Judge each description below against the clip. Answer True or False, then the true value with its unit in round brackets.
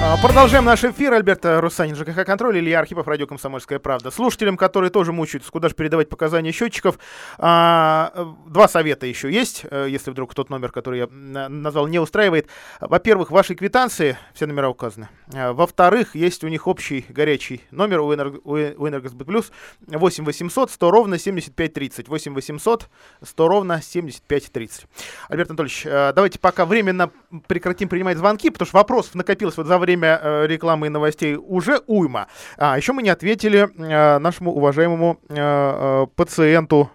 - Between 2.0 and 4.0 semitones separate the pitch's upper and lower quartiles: False (4.5 semitones)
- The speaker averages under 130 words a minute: False (150 wpm)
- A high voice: False (165 Hz)